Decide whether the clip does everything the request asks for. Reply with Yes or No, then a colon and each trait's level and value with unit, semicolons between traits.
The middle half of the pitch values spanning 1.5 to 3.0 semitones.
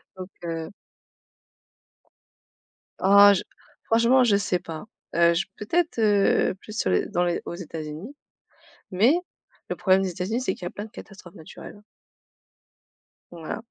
No: average, 3.8 semitones